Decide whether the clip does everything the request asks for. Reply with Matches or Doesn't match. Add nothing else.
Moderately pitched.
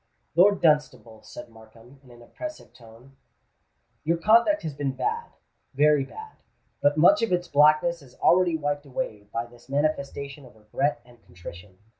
Matches